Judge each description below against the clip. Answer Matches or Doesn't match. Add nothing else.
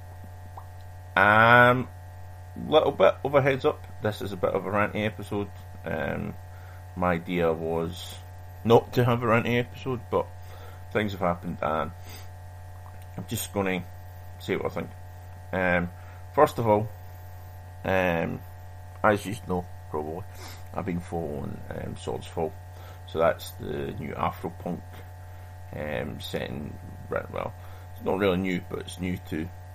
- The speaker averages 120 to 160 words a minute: Matches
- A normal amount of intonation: Doesn't match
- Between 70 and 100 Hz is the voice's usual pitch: Matches